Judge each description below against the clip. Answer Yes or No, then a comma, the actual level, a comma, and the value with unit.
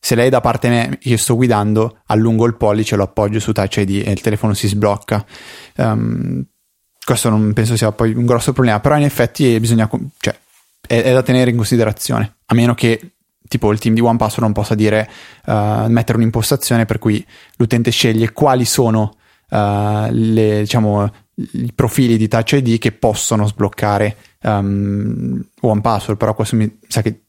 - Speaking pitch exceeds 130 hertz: No, low, 110 Hz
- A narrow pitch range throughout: Yes, narrow, 2.1 semitones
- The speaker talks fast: Yes, fast, 185 wpm